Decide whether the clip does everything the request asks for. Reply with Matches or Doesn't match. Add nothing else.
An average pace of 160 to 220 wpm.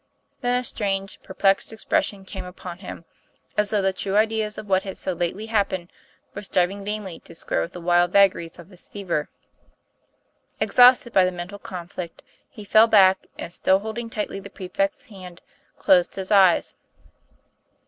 Matches